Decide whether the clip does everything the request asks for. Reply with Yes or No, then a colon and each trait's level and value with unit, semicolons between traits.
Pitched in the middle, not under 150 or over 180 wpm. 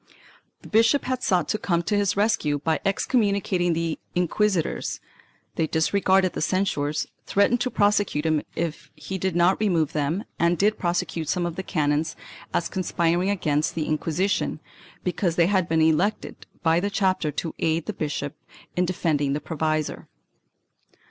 Yes: medium, 175 Hz; average, 160 wpm